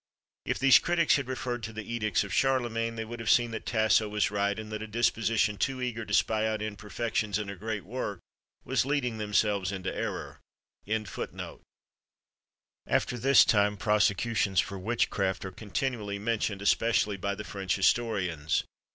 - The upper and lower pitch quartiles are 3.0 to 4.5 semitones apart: No, narrow, 2.6 semitones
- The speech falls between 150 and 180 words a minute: Yes, average, 160 wpm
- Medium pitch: No, low, 110 Hz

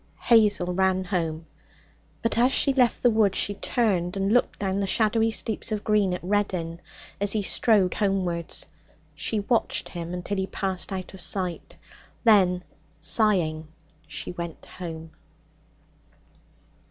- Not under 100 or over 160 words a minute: Yes, average, 140 wpm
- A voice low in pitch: No, high, 190 Hz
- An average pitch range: Yes, average, 3.3 semitones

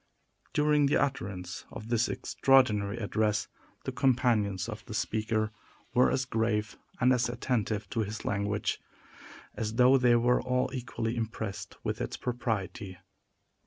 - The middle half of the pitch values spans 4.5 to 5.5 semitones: No, average, 3.0 semitones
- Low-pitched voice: Yes, low, 115 Hz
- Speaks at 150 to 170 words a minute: No, slow, 135 wpm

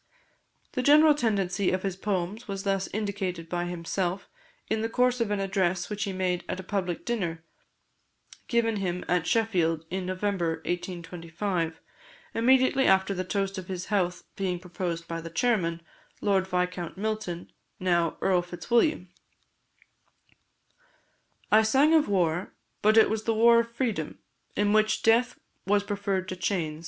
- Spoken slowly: No, average, 150 wpm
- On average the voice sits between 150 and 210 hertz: Yes, high, 190 Hz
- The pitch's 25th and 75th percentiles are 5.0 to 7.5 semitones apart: No, average, 3.5 semitones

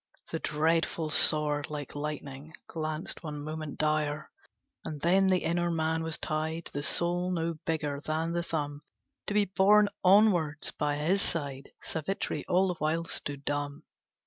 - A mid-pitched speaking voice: Yes, medium, 160 Hz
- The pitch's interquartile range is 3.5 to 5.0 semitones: No, narrow, 2.5 semitones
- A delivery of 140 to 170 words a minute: Yes, average, 150 wpm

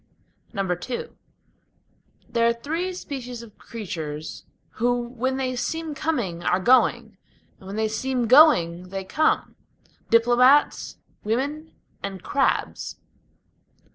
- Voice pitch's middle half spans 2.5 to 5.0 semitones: No, wide, 5.4 semitones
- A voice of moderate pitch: No, high, 240 Hz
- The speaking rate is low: Yes, slow, 105 wpm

